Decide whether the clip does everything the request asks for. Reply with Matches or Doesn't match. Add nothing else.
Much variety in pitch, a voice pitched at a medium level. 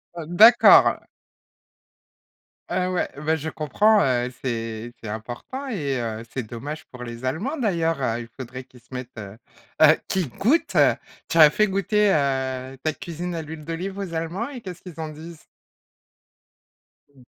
Matches